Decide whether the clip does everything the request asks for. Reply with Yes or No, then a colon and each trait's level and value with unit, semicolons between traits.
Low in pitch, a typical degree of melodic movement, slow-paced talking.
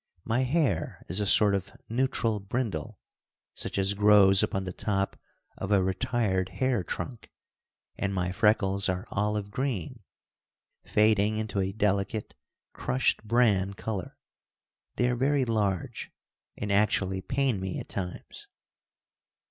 Yes: low, 105 Hz; average, 3.2 semitones; slow, 130 wpm